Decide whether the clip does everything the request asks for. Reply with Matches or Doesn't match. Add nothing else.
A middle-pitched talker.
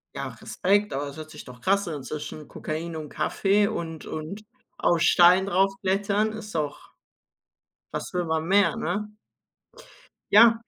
Matches